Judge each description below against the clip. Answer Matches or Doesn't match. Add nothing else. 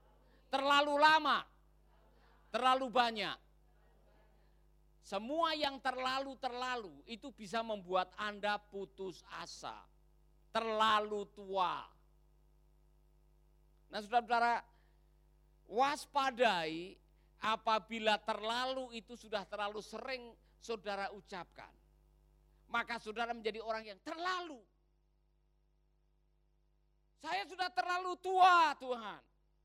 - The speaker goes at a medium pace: Doesn't match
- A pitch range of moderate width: Doesn't match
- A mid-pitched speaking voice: Doesn't match